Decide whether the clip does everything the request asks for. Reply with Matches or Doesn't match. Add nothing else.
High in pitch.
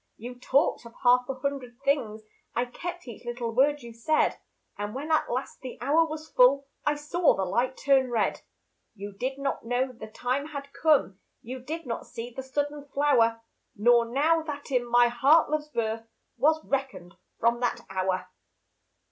Matches